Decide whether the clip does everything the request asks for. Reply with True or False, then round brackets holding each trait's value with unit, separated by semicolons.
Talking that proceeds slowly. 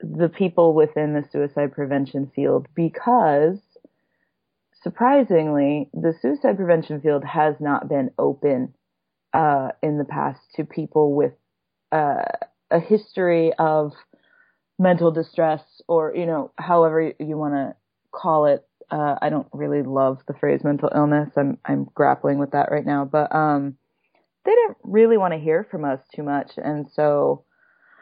False (150 wpm)